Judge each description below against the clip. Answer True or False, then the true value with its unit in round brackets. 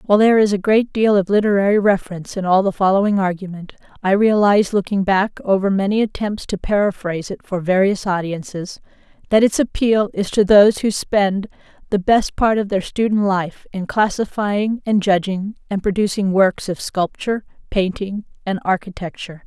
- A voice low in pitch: False (200 Hz)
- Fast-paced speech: False (165 wpm)